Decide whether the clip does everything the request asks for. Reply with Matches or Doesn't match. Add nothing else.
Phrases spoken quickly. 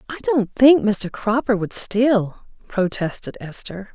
Doesn't match